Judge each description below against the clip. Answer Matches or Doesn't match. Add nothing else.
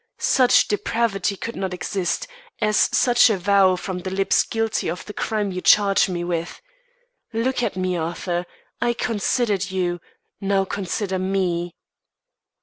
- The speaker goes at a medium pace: Matches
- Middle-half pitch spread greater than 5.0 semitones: Doesn't match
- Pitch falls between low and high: Doesn't match